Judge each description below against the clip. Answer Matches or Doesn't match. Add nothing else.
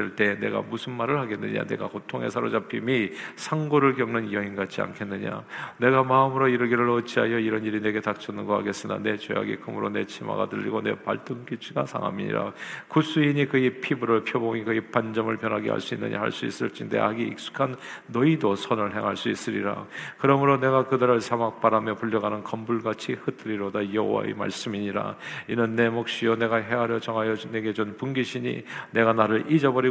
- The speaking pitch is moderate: Doesn't match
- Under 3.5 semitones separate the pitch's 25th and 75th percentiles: Matches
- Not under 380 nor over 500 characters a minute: Matches